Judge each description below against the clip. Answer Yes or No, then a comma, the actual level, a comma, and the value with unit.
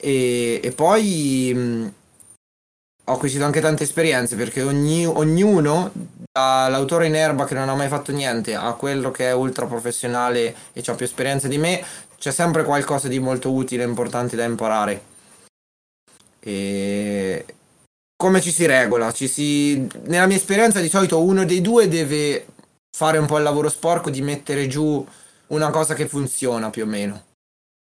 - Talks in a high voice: No, medium, 140 Hz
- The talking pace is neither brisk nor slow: Yes, average, 160 wpm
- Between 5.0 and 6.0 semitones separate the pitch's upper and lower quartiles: No, average, 4.5 semitones